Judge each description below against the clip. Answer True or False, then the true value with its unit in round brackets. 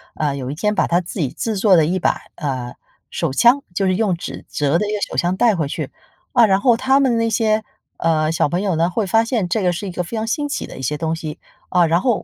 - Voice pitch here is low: False (185 Hz)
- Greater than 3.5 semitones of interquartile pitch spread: True (5.4 semitones)